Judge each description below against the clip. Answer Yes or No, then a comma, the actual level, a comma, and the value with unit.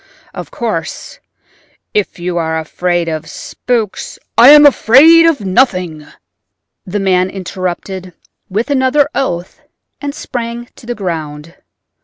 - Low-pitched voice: No, high, 195 Hz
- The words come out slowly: Yes, slow, 120 wpm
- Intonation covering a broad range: Yes, wide, 6.2 semitones